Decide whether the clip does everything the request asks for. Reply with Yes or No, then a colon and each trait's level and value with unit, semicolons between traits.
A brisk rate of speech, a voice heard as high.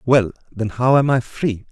No: fast, 210 wpm; low, 120 Hz